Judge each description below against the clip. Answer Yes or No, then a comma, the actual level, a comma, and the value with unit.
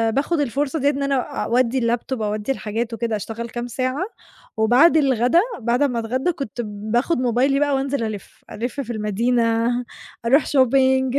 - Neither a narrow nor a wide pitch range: Yes, average, 3.1 semitones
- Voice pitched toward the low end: No, high, 245 Hz